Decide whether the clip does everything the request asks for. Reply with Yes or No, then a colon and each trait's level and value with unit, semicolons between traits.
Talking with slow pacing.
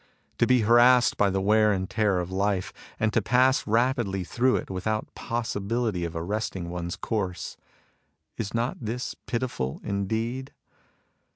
No: average, 150 wpm